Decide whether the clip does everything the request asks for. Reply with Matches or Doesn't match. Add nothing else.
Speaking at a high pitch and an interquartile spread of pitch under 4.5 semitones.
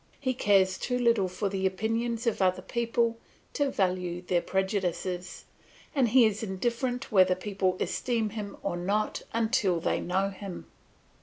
Matches